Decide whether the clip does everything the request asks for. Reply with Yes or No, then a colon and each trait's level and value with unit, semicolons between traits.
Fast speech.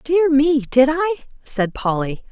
No: average, 155 wpm